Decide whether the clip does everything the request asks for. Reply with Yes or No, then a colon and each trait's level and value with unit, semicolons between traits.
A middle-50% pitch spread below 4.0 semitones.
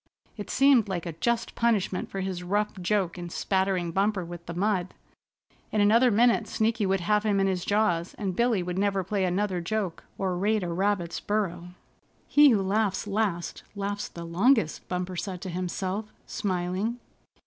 Yes: average, 2.9 semitones